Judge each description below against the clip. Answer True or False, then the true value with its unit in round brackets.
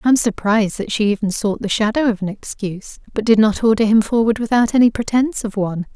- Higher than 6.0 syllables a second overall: True (6.3 syllables/s)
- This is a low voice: False (220 Hz)